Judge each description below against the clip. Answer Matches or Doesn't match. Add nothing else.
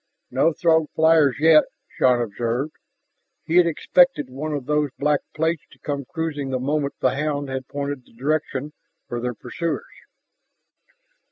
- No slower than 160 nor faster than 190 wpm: Doesn't match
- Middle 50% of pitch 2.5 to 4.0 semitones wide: Matches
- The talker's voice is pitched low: Doesn't match